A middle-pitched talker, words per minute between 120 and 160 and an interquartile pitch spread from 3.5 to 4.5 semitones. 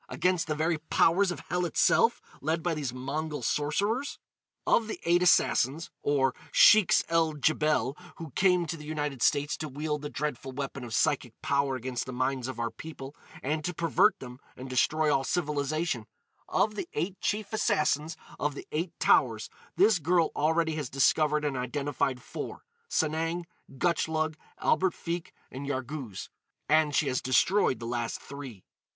Yes: medium, 150 Hz; average, 155 wpm; average, 3.9 semitones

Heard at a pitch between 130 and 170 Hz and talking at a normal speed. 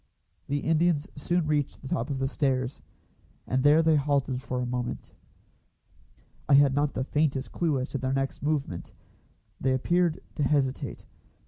Yes: medium, 140 Hz; average, 160 wpm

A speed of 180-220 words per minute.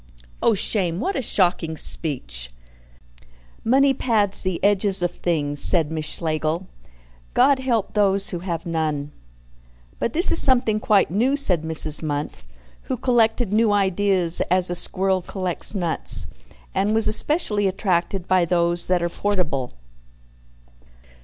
No: slow, 135 wpm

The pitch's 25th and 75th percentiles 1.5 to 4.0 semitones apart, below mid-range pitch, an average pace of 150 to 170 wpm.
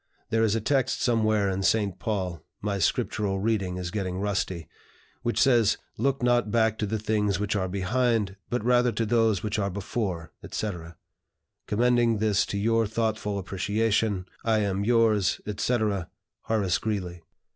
Yes: narrow, 2.6 semitones; low, 105 Hz; average, 155 wpm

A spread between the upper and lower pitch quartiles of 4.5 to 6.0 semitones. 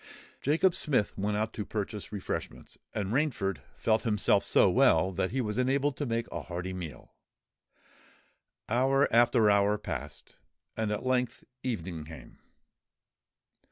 Yes: average, 5.2 semitones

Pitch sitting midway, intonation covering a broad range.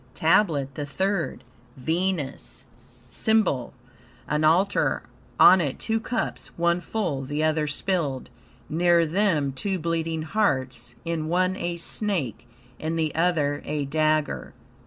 No: medium, 160 Hz; average, 3.9 semitones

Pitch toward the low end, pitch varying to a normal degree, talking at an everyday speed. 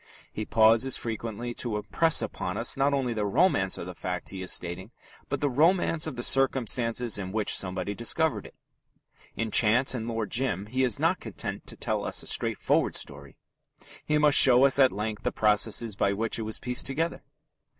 Yes: low, 115 Hz; average, 4.3 semitones; average, 190 wpm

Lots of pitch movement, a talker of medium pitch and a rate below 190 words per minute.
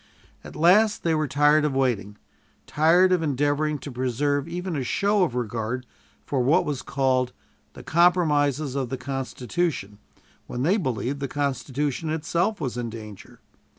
No: average, 4.1 semitones; medium, 145 Hz; average, 150 wpm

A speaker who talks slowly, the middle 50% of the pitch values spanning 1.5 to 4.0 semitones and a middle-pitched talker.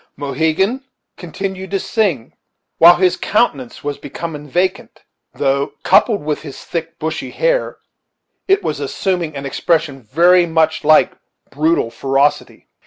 No: slow, 125 wpm; average, 4.5 semitones; medium, 160 Hz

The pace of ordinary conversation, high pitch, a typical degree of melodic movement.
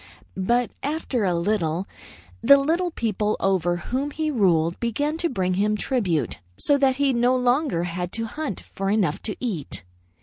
No: average, 165 wpm; high, 220 Hz; wide, 6.9 semitones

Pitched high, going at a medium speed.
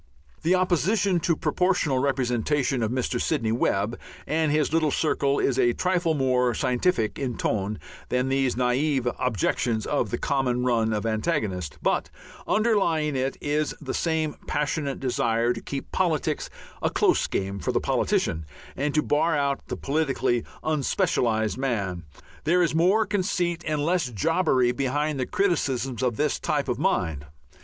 No: medium, 140 Hz; average, 150 wpm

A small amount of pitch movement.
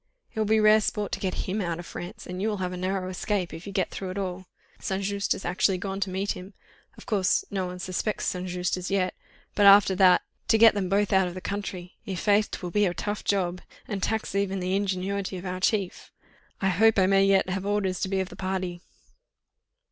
Yes: narrow, 1.7 semitones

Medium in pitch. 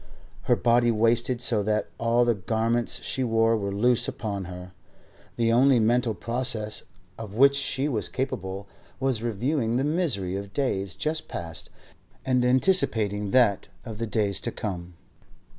No: low, 115 Hz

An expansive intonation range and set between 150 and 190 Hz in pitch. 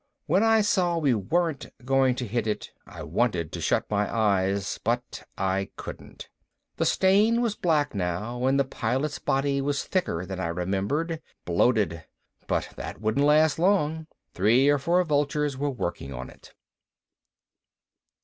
No: wide, 7.5 semitones; low, 135 Hz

